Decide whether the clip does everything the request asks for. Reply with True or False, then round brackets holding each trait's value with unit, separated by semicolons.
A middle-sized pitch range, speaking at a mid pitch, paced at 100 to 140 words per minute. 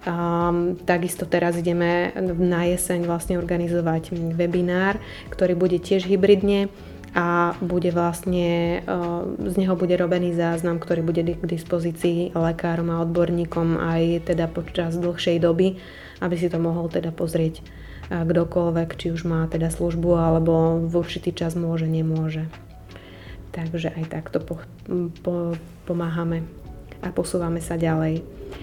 False (1.1 semitones; 170 Hz; 130 wpm)